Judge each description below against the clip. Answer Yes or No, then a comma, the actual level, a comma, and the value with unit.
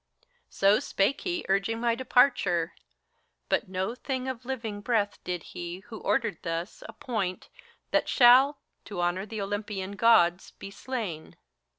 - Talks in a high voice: Yes, high, 205 Hz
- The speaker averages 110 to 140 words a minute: Yes, slow, 135 wpm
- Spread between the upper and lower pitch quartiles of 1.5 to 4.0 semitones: No, average, 4.5 semitones